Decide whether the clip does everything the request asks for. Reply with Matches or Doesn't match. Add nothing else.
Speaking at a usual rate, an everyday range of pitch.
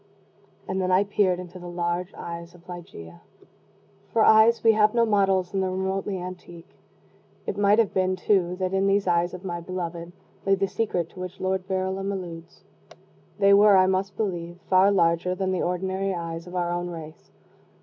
Doesn't match